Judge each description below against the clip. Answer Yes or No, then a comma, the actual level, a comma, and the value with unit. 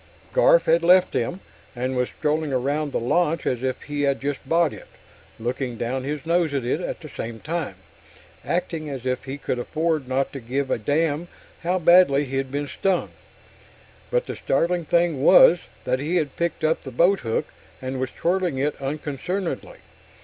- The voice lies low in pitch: No, medium, 145 Hz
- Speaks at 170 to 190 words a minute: Yes, average, 180 wpm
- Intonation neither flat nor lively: Yes, average, 4.4 semitones